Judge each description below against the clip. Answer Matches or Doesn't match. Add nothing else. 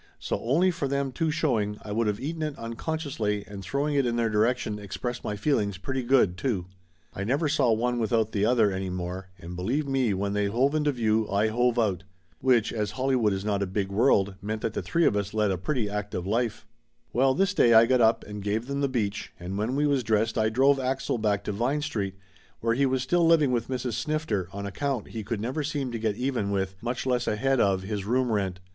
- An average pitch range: Matches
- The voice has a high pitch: Doesn't match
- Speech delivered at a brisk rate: Matches